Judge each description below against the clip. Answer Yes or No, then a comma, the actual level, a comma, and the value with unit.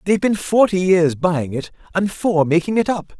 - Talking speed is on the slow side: No, fast, 205 wpm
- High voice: No, medium, 180 Hz